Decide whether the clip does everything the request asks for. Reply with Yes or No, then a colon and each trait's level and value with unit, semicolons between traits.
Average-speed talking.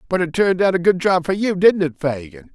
No: fast, 285 wpm